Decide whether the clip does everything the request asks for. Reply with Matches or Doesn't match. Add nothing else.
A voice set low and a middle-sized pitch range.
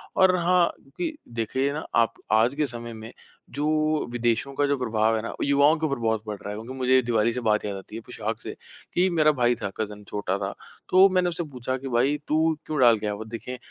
Matches